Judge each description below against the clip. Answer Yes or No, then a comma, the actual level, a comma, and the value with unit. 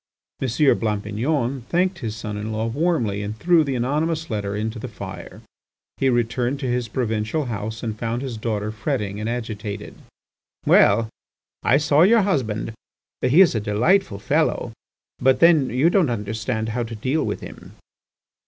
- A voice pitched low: Yes, low, 115 Hz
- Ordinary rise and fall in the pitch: Yes, average, 4.4 semitones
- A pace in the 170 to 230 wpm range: No, average, 160 wpm